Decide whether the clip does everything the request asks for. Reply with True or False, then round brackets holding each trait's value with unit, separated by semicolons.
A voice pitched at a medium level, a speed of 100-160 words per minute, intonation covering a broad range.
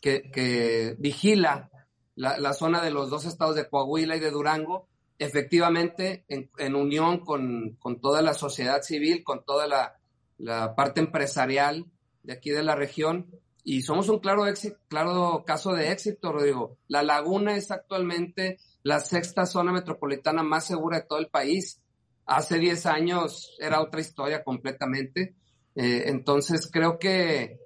False (155 Hz; 155 wpm; 3.8 semitones)